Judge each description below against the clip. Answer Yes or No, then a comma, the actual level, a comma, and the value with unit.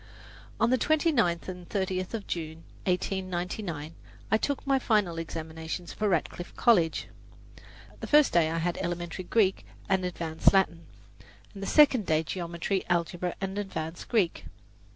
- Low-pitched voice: No, medium, 180 Hz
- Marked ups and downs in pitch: No, average, 3.5 semitones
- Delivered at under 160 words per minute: Yes, average, 140 wpm